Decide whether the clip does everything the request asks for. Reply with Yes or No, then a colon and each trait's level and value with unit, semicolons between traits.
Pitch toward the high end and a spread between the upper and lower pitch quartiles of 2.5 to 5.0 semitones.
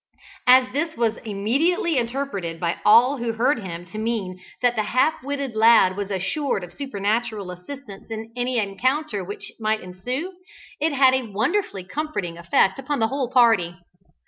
No: high, 230 Hz; wide, 5.4 semitones